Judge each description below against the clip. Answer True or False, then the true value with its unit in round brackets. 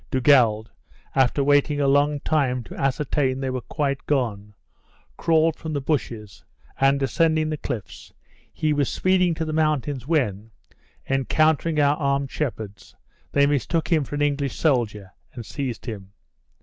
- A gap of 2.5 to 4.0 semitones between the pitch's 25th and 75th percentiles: True (3.4 semitones)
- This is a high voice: False (140 Hz)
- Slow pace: False (150 wpm)